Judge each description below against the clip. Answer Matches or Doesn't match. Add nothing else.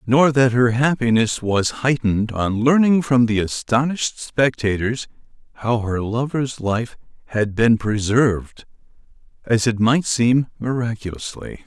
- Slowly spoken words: Matches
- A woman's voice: Doesn't match